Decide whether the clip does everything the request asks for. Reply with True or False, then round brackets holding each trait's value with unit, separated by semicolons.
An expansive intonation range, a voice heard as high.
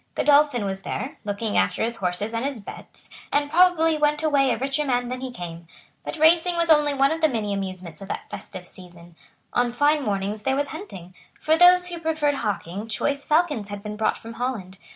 True (6.8 semitones; 250 Hz)